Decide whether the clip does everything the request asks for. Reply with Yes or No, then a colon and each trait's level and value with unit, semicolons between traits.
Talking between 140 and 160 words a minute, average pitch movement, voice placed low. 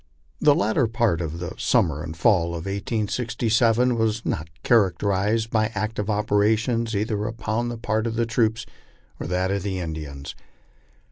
Yes: average, 150 wpm; average, 3.4 semitones; low, 110 Hz